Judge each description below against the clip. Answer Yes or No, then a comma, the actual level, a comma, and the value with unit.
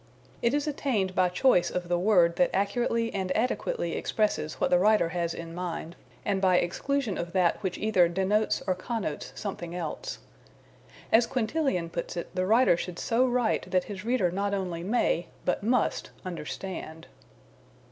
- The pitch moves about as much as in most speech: Yes, average, 4.6 semitones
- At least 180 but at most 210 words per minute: No, average, 165 wpm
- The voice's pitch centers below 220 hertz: Yes, high, 190 Hz